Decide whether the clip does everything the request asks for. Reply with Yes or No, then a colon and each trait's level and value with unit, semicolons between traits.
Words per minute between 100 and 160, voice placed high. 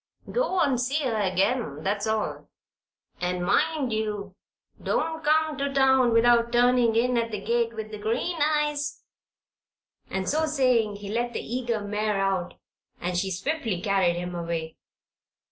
Yes: average, 150 wpm; high, 230 Hz